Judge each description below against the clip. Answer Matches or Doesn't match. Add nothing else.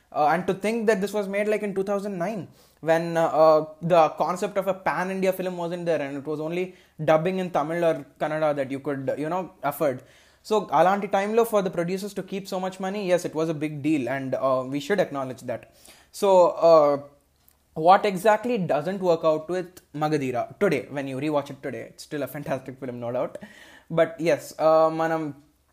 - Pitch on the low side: Doesn't match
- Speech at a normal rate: Doesn't match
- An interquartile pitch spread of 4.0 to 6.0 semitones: Matches